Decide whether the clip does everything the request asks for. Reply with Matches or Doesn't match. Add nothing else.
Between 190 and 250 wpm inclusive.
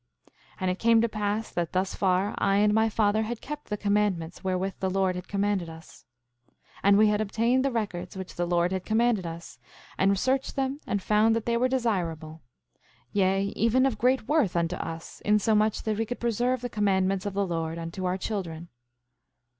Matches